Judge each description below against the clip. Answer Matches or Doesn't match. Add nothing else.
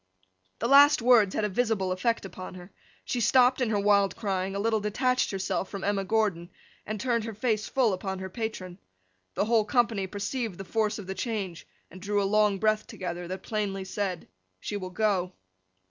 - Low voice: Doesn't match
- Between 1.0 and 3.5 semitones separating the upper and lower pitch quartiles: Matches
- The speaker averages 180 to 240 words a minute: Matches